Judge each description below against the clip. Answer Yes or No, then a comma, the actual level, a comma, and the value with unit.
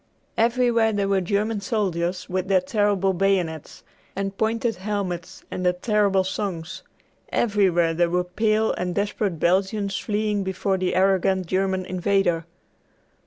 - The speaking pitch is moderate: No, high, 195 Hz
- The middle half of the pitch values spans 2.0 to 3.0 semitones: Yes, narrow, 2.4 semitones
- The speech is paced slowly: Yes, slow, 130 wpm